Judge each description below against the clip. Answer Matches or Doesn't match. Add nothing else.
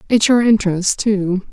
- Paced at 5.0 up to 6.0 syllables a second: Doesn't match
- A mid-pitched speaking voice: Doesn't match